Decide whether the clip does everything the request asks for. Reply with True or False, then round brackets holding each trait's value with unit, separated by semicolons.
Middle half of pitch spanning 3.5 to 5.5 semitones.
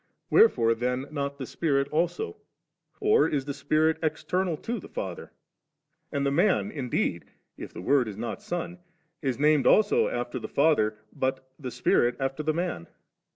True (4.6 semitones)